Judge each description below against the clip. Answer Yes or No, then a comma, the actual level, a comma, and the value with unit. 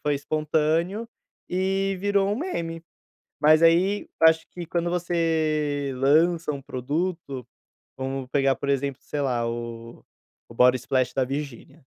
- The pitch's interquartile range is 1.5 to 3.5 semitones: No, average, 4.2 semitones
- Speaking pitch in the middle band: Yes, medium, 150 Hz